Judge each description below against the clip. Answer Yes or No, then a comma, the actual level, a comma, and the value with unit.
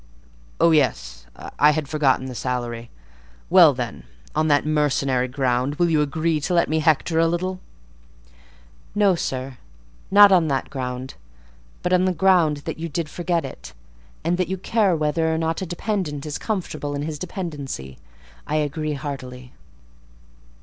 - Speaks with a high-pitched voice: No, medium, 150 Hz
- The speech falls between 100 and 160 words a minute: Yes, average, 155 wpm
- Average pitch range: Yes, average, 4.2 semitones